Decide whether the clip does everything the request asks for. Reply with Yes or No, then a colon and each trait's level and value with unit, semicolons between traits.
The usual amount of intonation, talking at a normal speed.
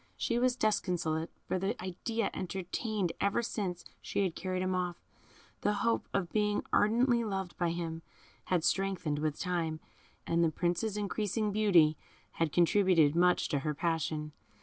Yes: average, 3.9 semitones; average, 150 wpm